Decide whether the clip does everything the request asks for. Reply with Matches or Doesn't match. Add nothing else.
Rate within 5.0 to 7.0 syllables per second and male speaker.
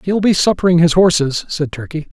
Matches